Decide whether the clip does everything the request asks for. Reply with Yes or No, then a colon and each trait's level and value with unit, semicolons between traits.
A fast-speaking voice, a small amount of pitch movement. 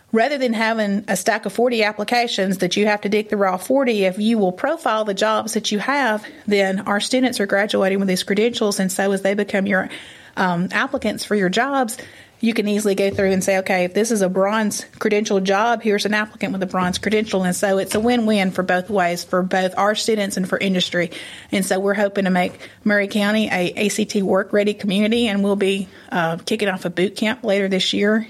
Yes: fast, 225 wpm; narrow, 2.2 semitones